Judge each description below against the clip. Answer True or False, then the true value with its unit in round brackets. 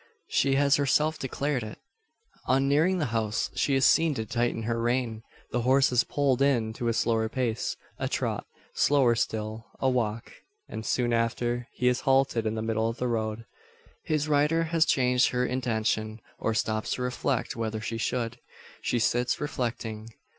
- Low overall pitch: True (120 Hz)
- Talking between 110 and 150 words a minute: False (175 wpm)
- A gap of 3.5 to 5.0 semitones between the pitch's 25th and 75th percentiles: False (3.1 semitones)